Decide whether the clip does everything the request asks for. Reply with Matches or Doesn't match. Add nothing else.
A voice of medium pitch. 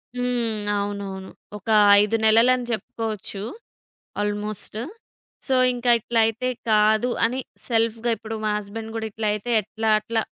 Doesn't match